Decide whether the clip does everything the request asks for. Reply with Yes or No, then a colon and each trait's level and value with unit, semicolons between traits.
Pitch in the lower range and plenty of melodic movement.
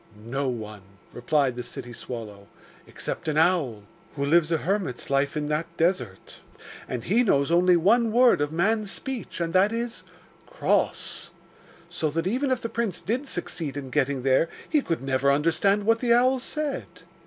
No: medium, 165 Hz; wide, 8.2 semitones